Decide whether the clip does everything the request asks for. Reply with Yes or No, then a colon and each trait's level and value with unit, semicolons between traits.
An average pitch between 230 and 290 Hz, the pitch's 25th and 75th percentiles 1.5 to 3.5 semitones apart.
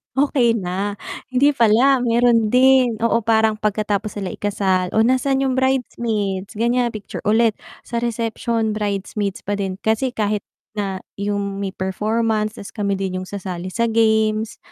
No: high, 220 Hz; average, 2.7 semitones